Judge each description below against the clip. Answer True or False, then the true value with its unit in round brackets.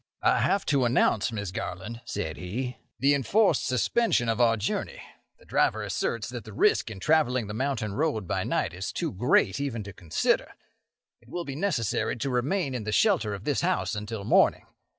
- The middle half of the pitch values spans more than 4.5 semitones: True (5.2 semitones)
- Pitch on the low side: True (120 Hz)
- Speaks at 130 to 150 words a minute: False (190 wpm)